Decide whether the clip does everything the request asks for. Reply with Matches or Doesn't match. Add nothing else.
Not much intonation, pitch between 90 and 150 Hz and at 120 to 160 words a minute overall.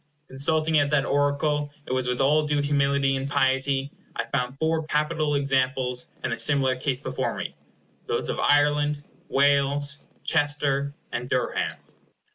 Matches